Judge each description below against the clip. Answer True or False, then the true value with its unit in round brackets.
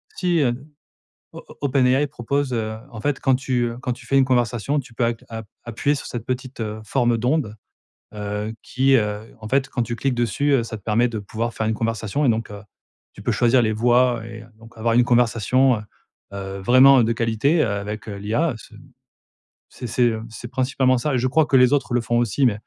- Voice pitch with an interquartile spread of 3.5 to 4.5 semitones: False (2.9 semitones)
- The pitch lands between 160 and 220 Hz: False (120 Hz)